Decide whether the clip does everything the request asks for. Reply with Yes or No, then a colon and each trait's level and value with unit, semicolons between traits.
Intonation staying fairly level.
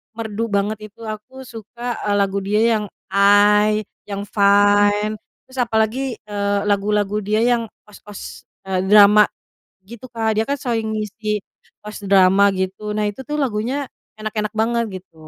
Yes: narrow, 1.8 semitones